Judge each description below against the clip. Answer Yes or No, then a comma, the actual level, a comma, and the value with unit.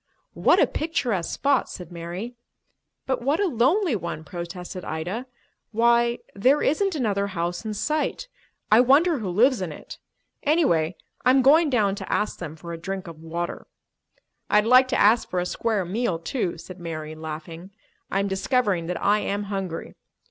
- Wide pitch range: Yes, wide, 6.6 semitones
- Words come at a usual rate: Yes, average, 170 wpm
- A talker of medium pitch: No, high, 200 Hz